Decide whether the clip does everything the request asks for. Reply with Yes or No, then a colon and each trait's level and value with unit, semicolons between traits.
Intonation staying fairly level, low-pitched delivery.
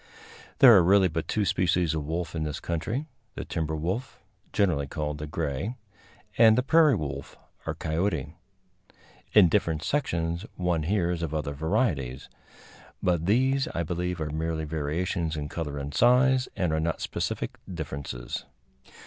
No: average, 4.2 semitones; very low, 85 Hz